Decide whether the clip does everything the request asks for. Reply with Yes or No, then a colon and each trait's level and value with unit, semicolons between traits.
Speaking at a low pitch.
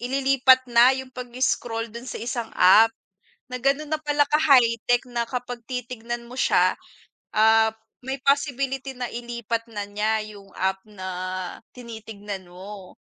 No: high, 240 Hz